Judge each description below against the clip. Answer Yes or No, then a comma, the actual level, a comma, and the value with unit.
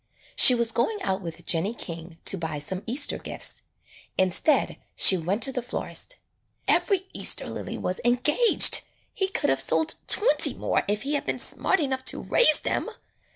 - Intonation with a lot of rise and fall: Yes, wide, 8.7 semitones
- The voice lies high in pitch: Yes, high, 235 Hz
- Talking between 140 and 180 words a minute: Yes, average, 170 wpm